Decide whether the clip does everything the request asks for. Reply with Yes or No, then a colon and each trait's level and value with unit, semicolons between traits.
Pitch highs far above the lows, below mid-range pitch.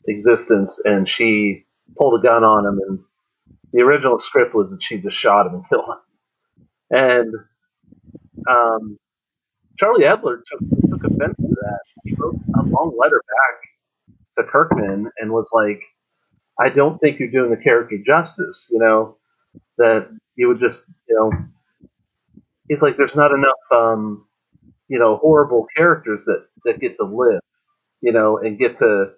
Yes: wide, 8.0 semitones; low, 120 Hz